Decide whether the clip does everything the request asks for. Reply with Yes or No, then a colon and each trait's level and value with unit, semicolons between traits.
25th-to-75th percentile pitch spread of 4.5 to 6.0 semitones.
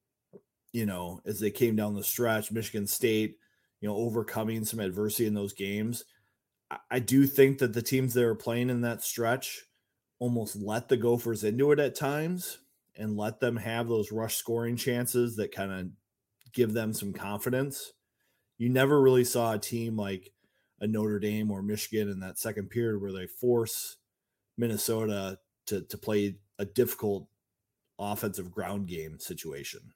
No: narrow, 2.6 semitones